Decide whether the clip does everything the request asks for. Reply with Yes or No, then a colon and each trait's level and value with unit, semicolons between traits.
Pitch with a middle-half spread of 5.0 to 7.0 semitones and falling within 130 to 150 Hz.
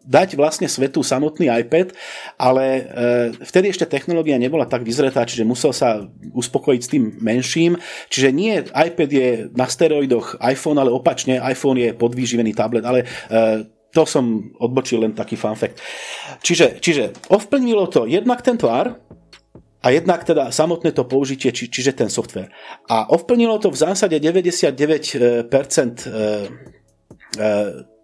Yes: wide, 5.6 semitones; low, 135 Hz